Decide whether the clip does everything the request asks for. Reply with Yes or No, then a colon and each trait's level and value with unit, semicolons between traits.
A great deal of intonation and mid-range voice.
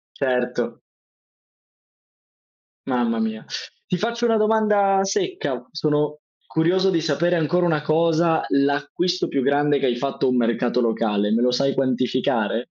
Yes: wide, 5.9 semitones; medium, 145 Hz